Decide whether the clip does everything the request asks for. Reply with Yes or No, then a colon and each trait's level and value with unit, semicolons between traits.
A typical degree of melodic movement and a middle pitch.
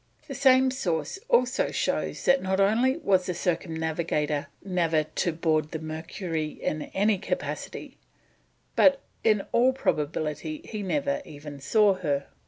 No: wide, 7.1 semitones; medium, 180 Hz